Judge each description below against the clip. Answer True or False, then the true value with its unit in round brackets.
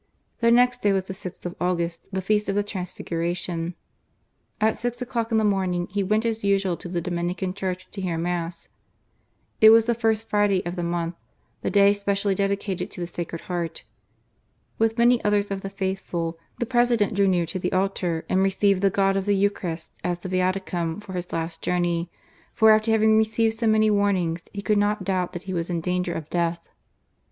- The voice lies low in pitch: False (190 Hz)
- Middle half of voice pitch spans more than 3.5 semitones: False (3.0 semitones)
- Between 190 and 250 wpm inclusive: True (200 wpm)